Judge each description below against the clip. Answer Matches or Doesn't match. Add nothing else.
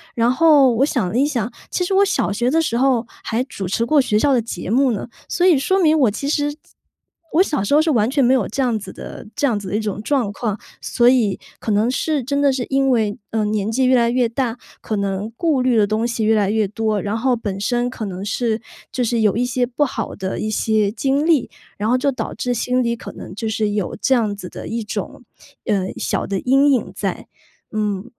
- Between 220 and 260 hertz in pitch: Matches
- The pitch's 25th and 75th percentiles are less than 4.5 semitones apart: Matches